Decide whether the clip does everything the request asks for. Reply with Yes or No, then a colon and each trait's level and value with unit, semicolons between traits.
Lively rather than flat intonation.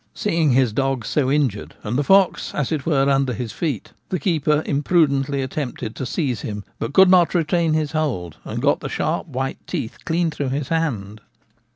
No: average, 4.0 semitones